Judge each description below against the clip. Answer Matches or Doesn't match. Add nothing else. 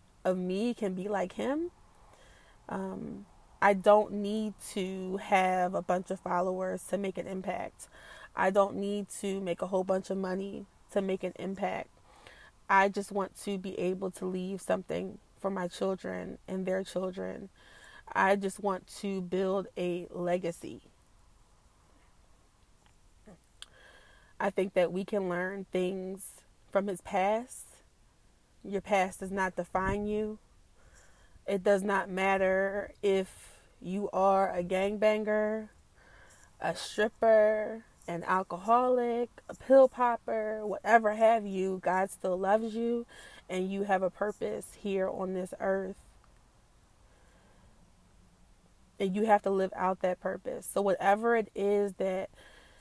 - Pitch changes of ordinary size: Doesn't match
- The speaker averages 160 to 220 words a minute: Doesn't match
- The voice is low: Doesn't match